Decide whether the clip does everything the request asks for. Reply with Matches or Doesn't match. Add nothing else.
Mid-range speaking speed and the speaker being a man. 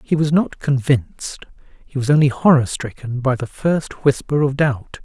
Matches